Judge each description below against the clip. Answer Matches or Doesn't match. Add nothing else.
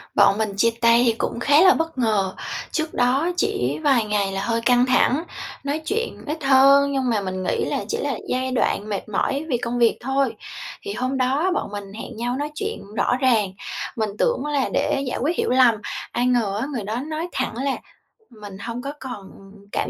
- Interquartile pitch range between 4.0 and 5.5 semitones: Matches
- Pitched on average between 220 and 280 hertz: Matches